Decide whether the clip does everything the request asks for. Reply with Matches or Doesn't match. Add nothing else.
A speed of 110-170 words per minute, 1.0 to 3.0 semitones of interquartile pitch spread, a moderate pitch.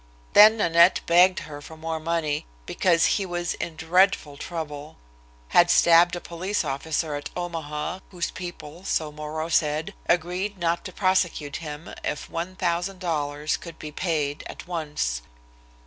Matches